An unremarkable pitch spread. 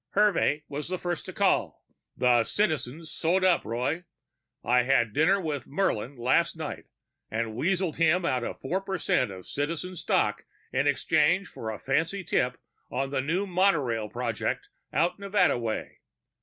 No: wide, 6.4 semitones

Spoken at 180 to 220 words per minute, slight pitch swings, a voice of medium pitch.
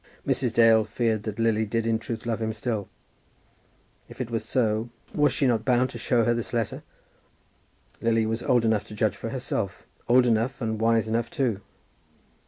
No: average, 185 wpm; narrow, 1.4 semitones; low, 115 Hz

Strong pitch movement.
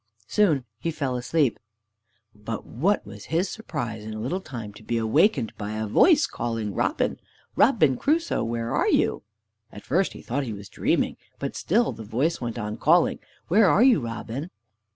Yes: wide, 7.8 semitones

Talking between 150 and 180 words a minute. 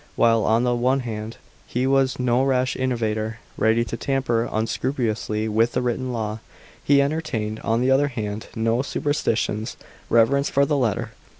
Yes: average, 160 wpm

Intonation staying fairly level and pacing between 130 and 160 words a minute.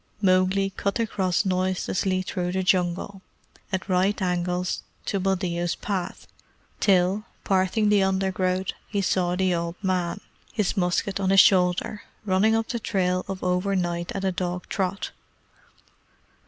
Yes: narrow, 1.4 semitones; slow, 135 wpm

